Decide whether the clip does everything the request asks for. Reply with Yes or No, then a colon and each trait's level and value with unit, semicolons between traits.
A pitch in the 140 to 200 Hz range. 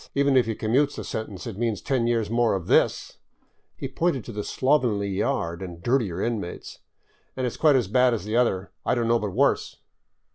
No: low, 115 Hz